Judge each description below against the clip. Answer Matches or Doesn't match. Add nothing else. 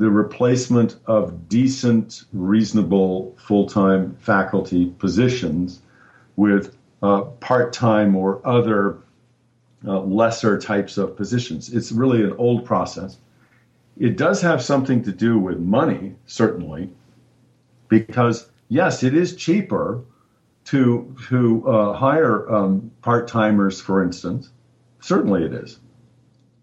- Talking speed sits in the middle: Doesn't match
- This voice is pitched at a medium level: Doesn't match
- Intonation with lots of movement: Doesn't match